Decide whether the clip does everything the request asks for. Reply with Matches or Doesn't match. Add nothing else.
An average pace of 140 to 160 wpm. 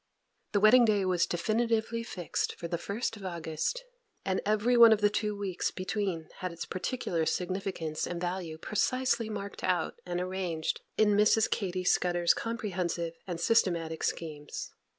Matches